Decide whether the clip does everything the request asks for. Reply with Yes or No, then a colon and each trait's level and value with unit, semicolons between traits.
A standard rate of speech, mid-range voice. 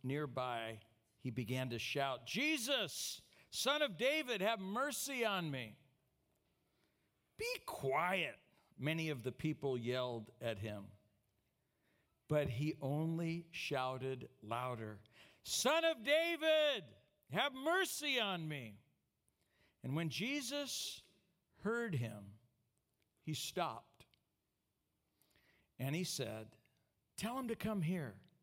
No: slow, 105 wpm; medium, 145 Hz